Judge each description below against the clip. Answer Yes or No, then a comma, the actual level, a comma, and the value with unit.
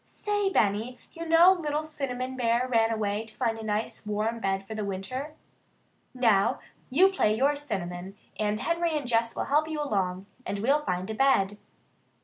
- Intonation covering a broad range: Yes, wide, 6.0 semitones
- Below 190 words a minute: Yes, average, 175 wpm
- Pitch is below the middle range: No, high, 230 Hz